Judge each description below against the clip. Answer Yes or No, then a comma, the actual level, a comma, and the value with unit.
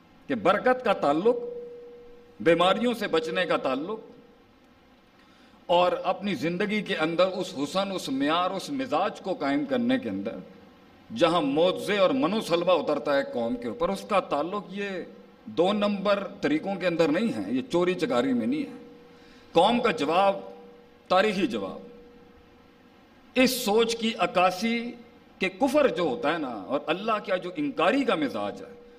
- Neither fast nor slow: Yes, average, 155 wpm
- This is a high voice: Yes, high, 240 Hz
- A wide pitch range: Yes, wide, 5.9 semitones